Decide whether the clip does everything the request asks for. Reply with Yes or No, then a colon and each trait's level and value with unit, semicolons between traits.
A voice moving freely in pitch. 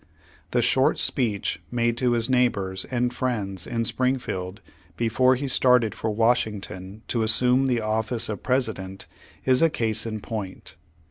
No: average, 3.1 semitones